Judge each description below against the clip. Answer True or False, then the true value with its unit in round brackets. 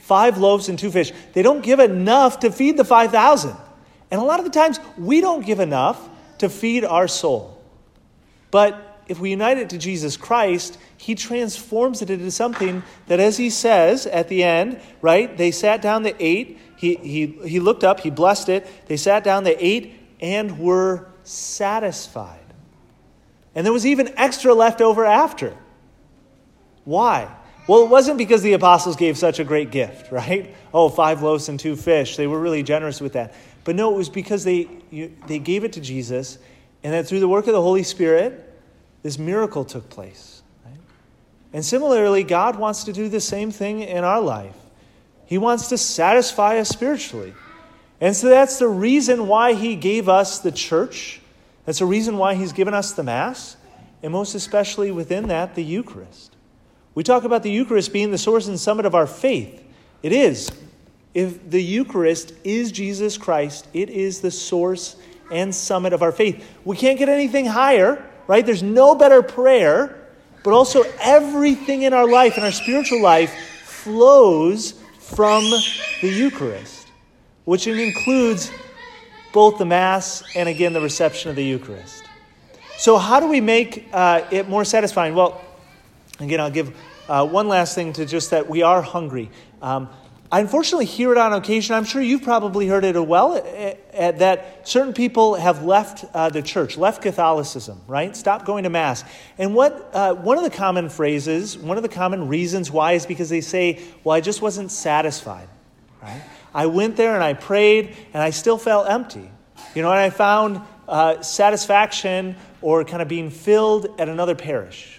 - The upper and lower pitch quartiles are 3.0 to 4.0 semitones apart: False (5.1 semitones)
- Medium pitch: False (195 Hz)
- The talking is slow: False (180 wpm)